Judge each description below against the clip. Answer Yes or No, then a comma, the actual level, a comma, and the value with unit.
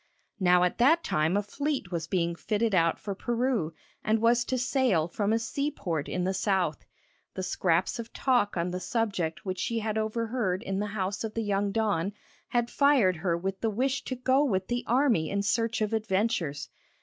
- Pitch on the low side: No, high, 205 Hz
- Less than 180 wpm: No, average, 195 wpm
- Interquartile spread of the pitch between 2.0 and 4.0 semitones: No, average, 4.4 semitones